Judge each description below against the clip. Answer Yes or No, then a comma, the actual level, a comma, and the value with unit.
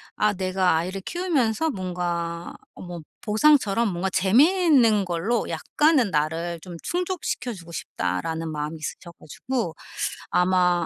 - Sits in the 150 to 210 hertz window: Yes, medium, 185 Hz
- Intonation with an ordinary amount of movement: No, wide, 5.9 semitones